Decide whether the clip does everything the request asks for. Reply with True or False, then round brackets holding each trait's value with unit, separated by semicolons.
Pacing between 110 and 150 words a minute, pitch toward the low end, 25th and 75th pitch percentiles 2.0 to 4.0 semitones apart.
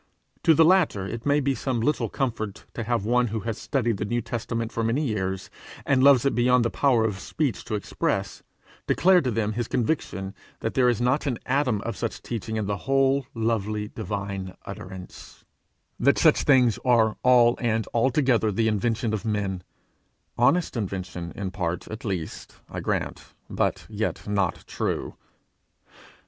False (170 wpm; 115 Hz; 3.5 semitones)